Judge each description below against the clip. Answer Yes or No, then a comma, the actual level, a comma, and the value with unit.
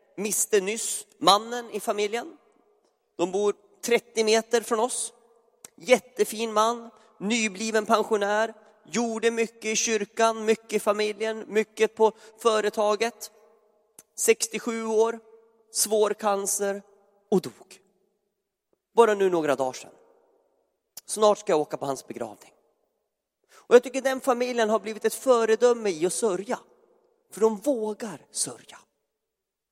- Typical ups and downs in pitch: No, narrow, 1.8 semitones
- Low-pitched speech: No, high, 220 Hz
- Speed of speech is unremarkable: No, slow, 120 wpm